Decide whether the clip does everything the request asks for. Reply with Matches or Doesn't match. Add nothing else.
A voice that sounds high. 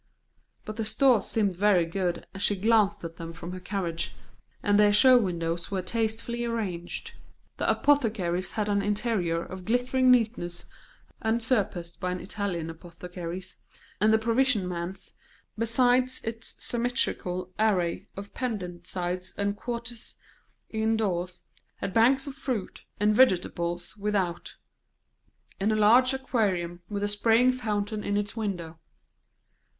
Matches